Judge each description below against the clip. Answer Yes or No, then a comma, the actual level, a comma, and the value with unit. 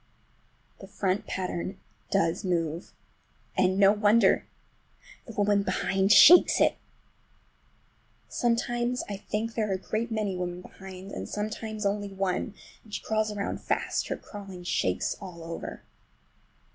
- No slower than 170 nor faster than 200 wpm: No, slow, 135 wpm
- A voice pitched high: Yes, high, 200 Hz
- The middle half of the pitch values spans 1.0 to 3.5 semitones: Yes, narrow, 2.6 semitones